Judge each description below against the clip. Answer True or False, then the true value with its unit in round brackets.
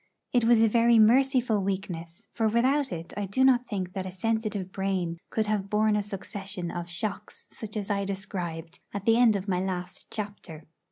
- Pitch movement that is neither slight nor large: True (3.3 semitones)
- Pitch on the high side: True (200 Hz)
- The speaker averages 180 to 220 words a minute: True (190 wpm)